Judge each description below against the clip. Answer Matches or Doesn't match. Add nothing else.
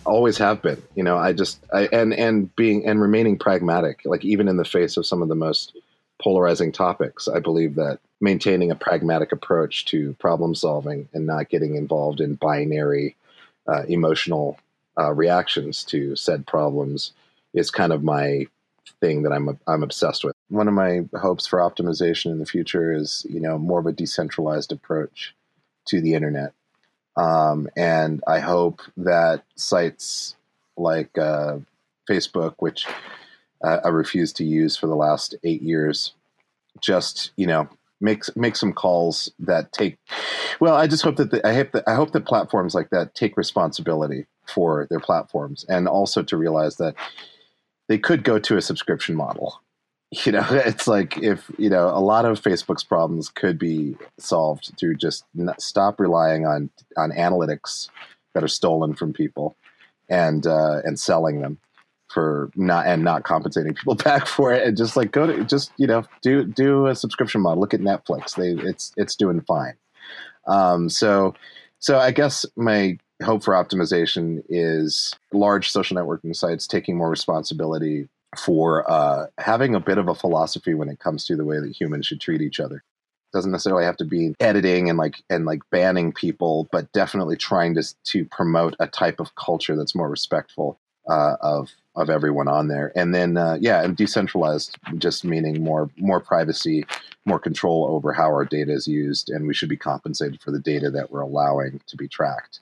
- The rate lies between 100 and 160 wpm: Doesn't match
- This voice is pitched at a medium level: Doesn't match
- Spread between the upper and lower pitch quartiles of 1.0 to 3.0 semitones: Doesn't match